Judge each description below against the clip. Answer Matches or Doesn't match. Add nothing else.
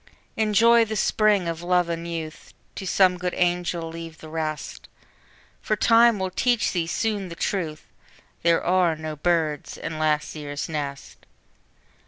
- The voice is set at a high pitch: Doesn't match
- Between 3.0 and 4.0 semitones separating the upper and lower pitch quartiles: Matches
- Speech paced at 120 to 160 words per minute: Matches